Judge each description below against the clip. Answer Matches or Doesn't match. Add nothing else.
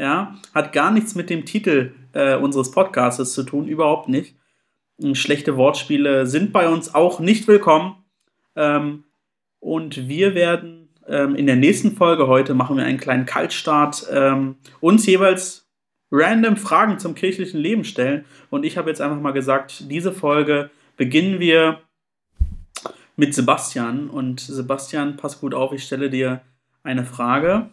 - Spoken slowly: Doesn't match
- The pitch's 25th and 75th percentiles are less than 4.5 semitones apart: Doesn't match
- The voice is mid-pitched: Matches